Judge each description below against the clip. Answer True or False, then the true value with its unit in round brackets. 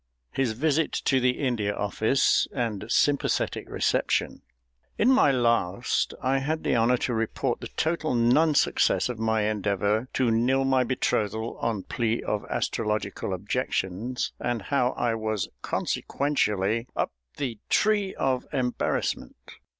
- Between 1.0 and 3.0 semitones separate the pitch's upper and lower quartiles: False (3.7 semitones)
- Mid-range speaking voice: False (120 Hz)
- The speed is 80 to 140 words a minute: True (135 wpm)